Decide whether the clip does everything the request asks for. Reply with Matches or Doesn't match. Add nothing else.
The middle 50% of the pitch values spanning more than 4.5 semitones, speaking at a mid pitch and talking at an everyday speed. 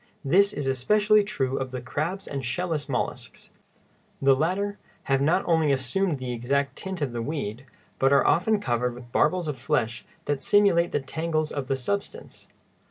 Matches